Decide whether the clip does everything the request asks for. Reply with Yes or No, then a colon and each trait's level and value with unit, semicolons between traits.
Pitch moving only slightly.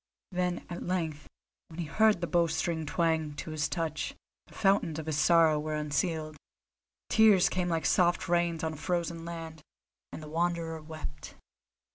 Yes: narrow, 1.8 semitones